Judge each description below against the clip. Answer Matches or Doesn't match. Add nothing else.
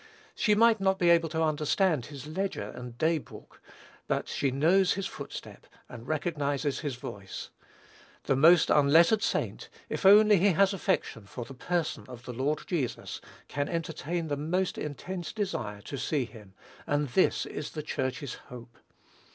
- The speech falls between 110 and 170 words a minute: Matches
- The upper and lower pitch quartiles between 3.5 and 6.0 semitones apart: Matches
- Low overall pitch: Doesn't match